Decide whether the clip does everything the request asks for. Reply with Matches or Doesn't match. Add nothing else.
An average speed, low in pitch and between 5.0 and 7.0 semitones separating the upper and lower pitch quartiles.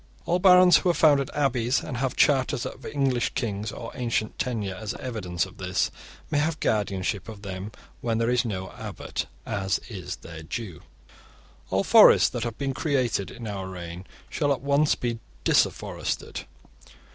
Matches